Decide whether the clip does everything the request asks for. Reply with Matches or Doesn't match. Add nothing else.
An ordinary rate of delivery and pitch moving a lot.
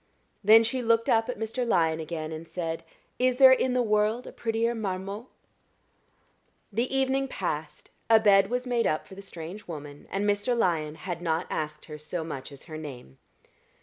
Matches